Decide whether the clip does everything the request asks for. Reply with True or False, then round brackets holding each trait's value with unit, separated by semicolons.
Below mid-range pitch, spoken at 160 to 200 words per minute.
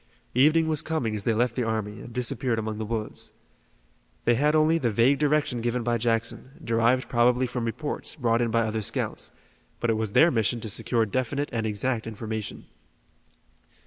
True (120 Hz; 180 wpm)